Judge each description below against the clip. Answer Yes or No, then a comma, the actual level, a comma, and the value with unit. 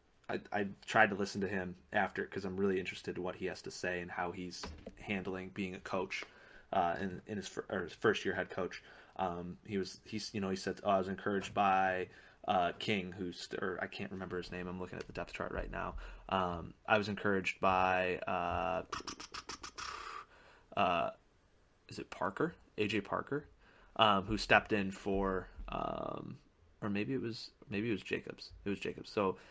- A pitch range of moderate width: No, narrow, 1.9 semitones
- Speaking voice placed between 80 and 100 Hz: Yes, very low, 95 Hz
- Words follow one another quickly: No, average, 195 wpm